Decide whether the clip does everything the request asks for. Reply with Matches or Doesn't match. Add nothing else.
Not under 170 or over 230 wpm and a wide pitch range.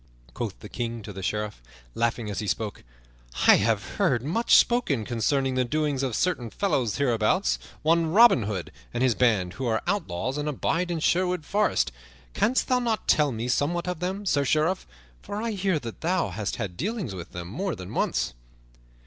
Matches